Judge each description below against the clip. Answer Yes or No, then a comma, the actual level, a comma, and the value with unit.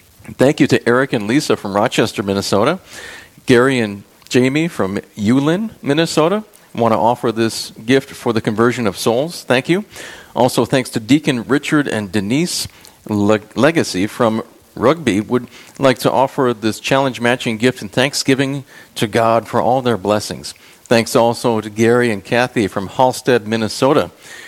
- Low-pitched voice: Yes, low, 120 Hz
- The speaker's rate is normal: Yes, average, 150 wpm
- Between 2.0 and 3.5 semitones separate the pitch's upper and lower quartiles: Yes, average, 3.2 semitones